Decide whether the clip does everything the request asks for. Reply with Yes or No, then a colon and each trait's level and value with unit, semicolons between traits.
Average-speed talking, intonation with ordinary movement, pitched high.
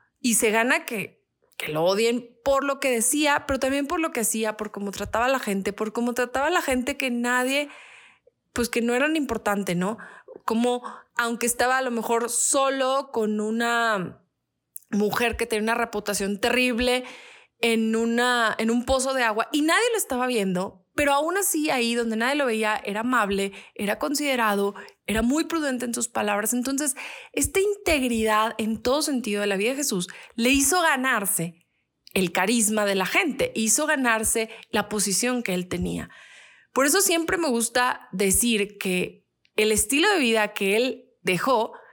Yes: average, 175 wpm; average, 4.0 semitones; high, 235 Hz